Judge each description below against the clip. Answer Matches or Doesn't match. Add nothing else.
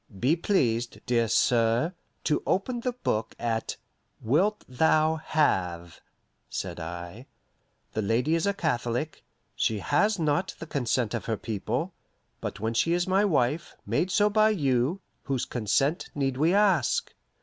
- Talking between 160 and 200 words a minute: Doesn't match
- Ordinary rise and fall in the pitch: Doesn't match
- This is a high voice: Doesn't match